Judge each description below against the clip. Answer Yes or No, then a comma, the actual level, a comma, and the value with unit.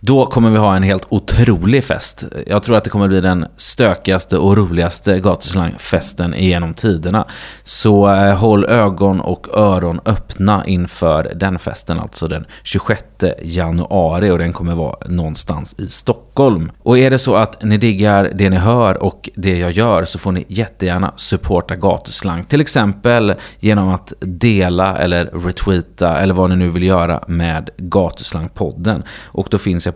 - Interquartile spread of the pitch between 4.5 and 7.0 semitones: No, average, 2.9 semitones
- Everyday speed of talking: Yes, average, 160 wpm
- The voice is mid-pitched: No, very low, 95 Hz